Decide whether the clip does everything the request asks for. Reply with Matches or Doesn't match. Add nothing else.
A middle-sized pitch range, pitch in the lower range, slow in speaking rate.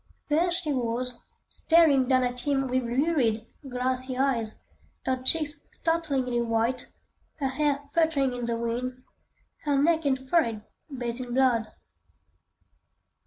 Doesn't match